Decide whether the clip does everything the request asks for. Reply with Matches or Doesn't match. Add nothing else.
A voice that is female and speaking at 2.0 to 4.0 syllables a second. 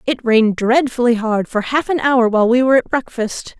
Doesn't match